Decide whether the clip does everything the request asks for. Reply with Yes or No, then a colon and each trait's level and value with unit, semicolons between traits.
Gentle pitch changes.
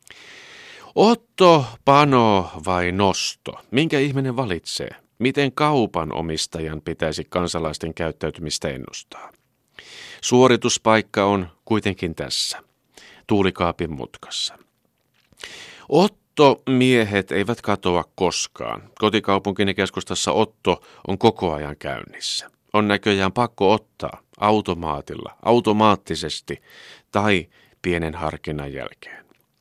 No: wide, 5.5 semitones